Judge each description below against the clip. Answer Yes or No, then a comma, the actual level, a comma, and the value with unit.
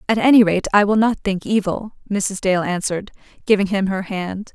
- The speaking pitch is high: Yes, high, 200 Hz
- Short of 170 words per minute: No, average, 200 wpm